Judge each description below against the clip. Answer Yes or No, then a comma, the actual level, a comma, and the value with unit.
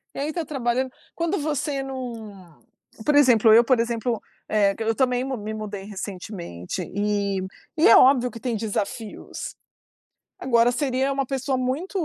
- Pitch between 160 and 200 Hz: No, high, 245 Hz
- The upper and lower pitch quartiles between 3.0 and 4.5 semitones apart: Yes, average, 4.0 semitones